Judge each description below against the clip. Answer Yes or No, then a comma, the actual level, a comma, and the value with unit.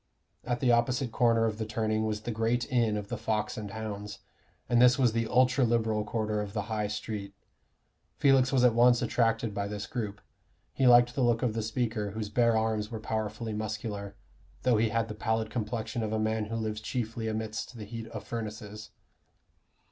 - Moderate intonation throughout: No, narrow, 1.8 semitones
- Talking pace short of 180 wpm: No, average, 195 wpm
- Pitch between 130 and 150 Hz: No, low, 110 Hz